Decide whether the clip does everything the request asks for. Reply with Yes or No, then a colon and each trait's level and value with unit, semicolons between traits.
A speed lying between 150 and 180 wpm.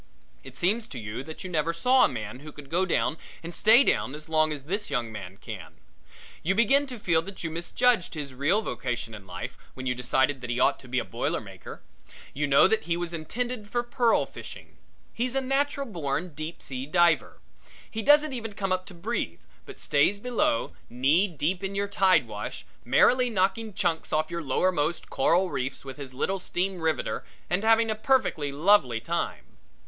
No: average, 200 wpm